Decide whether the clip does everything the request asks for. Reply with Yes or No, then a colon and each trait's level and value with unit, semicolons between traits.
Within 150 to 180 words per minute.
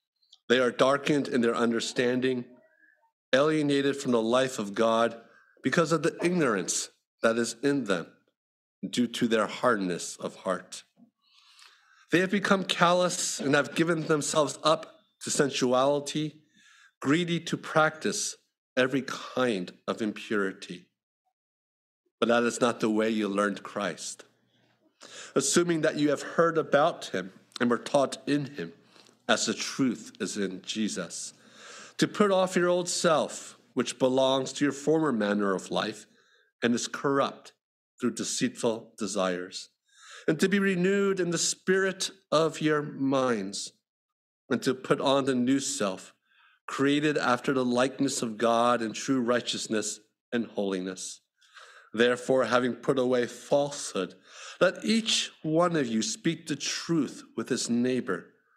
No: average, 140 wpm